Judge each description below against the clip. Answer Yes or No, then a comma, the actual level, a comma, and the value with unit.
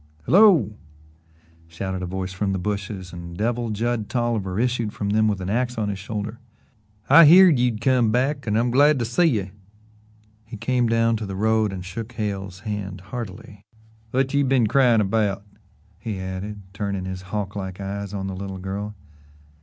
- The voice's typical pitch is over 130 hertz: No, low, 105 Hz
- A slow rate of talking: No, average, 175 wpm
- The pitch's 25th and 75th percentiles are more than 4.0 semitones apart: No, average, 3.6 semitones